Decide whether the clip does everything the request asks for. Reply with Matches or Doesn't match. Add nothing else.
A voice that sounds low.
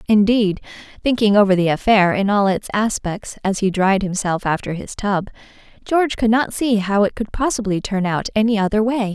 Doesn't match